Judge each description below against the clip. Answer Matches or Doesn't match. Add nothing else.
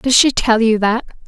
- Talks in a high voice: Matches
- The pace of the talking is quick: Matches